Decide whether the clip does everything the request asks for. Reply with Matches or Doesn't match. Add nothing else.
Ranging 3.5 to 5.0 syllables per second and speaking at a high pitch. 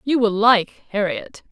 Matches